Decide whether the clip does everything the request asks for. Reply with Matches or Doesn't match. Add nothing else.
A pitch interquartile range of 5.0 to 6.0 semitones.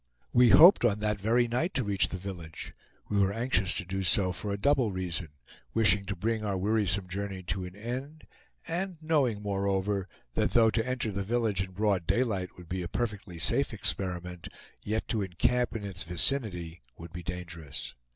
Doesn't match